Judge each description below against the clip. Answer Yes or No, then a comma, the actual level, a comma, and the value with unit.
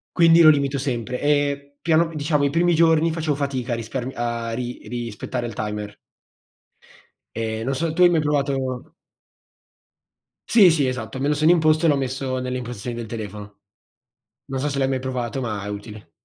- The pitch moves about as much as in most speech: Yes, average, 4.3 semitones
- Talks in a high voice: No, low, 135 Hz